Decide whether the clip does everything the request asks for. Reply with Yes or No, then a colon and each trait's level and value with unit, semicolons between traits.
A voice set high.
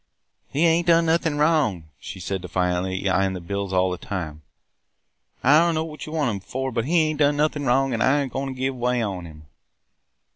No: low, 125 Hz